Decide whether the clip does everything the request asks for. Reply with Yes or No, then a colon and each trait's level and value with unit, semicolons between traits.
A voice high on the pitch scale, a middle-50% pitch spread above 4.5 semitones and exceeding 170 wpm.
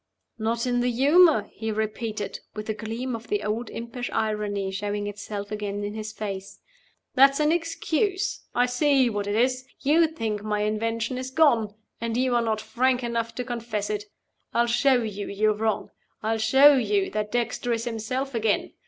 No: high, 230 Hz; average, 3.1 semitones; average, 180 wpm